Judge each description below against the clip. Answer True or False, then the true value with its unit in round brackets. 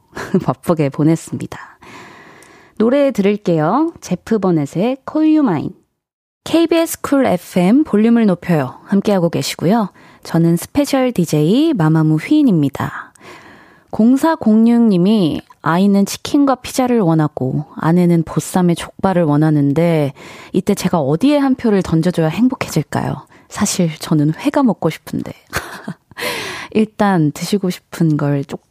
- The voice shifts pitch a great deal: True (7.1 semitones)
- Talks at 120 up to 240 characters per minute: False (275 characters per minute)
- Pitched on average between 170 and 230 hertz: True (185 Hz)